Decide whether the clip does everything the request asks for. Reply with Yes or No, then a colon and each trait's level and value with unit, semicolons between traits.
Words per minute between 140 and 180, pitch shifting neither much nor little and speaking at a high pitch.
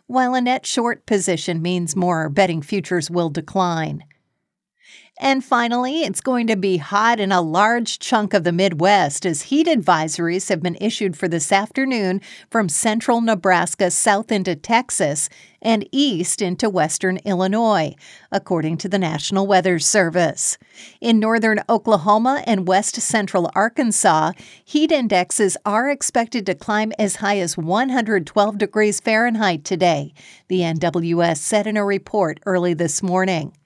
Yes: average, 145 wpm; average, 4.1 semitones; high, 200 Hz